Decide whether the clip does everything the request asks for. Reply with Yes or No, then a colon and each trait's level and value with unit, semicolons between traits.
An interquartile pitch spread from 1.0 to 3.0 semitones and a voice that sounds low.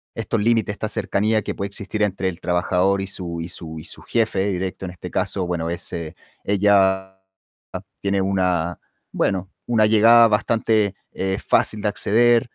Yes: average, 2.7 semitones; low, 100 Hz